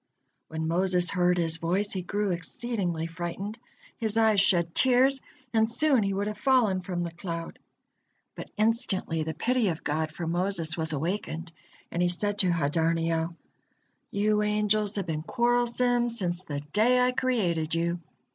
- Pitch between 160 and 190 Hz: Yes, medium, 185 Hz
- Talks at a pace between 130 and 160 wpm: Yes, average, 155 wpm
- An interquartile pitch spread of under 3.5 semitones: No, average, 4.5 semitones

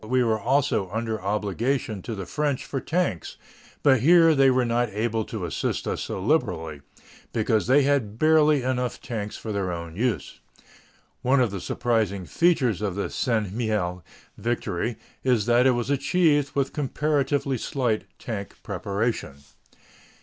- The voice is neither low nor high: No, low, 120 Hz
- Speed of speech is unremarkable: Yes, average, 150 wpm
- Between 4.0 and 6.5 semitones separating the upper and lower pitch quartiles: Yes, average, 4.8 semitones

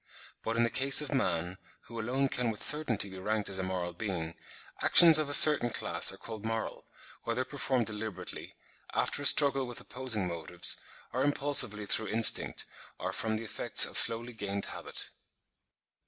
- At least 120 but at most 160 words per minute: No, average, 170 wpm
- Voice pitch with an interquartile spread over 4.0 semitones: Yes, average, 4.5 semitones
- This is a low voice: Yes, low, 115 Hz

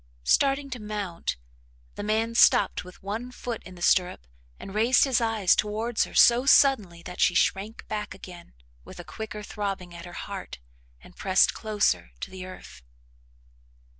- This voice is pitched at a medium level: No, high, 210 Hz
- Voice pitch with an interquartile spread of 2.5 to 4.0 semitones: Yes, average, 3.6 semitones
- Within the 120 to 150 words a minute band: No, average, 165 wpm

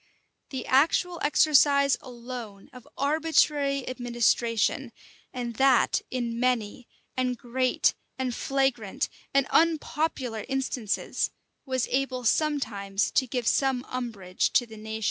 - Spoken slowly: Yes, slow, 110 wpm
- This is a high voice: Yes, very high, 255 Hz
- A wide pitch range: No, average, 2.8 semitones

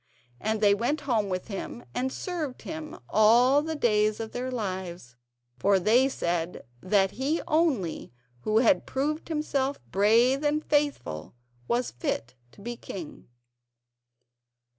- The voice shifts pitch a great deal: Yes, wide, 6.1 semitones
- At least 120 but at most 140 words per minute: Yes, slow, 135 wpm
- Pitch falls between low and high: No, high, 235 Hz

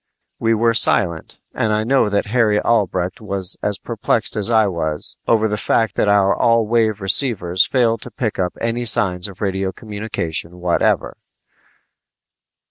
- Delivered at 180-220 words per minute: No, average, 155 wpm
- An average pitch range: Yes, average, 3.3 semitones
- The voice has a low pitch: Yes, low, 105 Hz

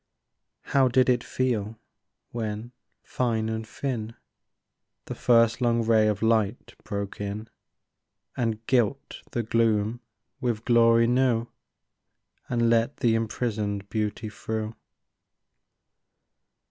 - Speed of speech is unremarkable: No, slow, 105 wpm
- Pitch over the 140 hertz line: No, low, 115 Hz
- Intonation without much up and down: Yes, narrow, 1.8 semitones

